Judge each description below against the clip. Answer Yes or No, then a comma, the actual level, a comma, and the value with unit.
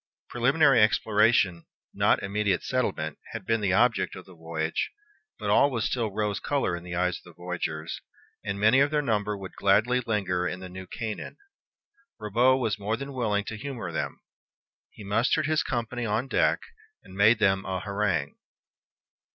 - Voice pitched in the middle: No, low, 105 Hz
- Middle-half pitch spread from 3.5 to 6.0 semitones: Yes, average, 4.2 semitones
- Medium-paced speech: Yes, average, 170 wpm